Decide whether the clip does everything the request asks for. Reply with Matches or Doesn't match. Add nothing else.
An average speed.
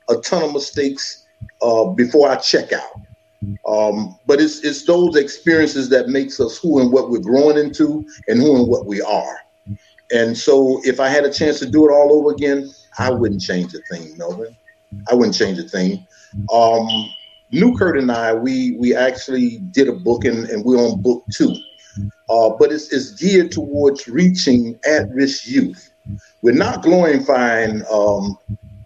Matches